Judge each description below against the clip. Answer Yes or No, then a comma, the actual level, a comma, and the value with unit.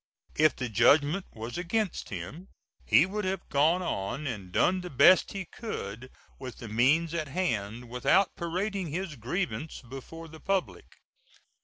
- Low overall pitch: No, medium, 155 Hz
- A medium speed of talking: Yes, average, 150 wpm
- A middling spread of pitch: No, wide, 6.9 semitones